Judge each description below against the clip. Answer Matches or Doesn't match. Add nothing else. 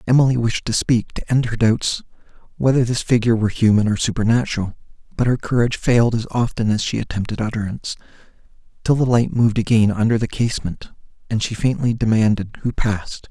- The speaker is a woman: Doesn't match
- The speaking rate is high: Doesn't match